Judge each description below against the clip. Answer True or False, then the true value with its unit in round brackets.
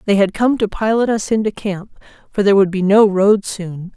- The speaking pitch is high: True (205 Hz)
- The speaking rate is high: True (225 wpm)